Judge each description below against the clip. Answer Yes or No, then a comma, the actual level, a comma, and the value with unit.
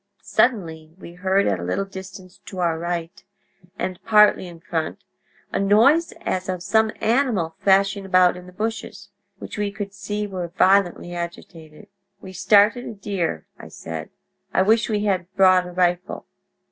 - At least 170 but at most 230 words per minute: No, average, 160 wpm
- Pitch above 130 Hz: Yes, high, 190 Hz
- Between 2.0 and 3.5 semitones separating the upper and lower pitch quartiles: Yes, average, 2.8 semitones